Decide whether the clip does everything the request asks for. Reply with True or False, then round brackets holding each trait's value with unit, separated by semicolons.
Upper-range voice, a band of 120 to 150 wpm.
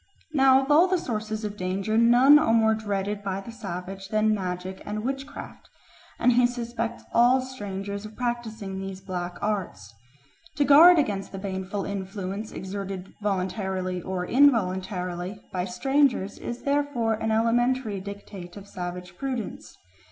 True (205 Hz; 140 wpm)